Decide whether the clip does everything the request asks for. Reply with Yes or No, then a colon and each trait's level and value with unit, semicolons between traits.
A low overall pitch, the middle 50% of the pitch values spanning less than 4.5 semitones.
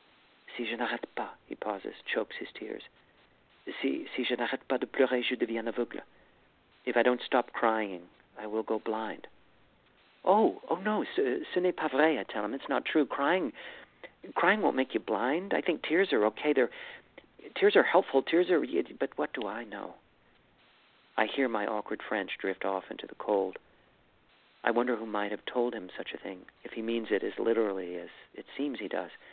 No: low, 120 Hz; wide, 5.5 semitones